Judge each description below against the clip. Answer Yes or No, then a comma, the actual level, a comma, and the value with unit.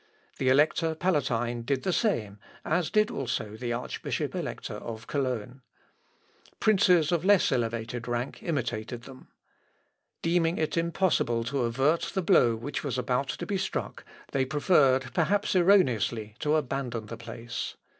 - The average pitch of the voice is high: No, low, 135 Hz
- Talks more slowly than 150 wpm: Yes, average, 140 wpm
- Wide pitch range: Yes, wide, 6.1 semitones